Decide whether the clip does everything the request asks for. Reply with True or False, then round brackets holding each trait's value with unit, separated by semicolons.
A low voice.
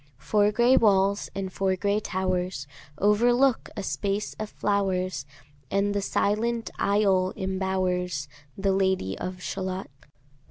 False (195 Hz)